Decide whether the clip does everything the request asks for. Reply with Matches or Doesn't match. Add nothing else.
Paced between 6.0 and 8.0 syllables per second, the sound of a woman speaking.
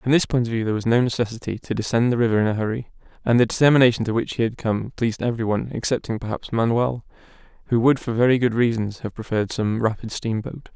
Doesn't match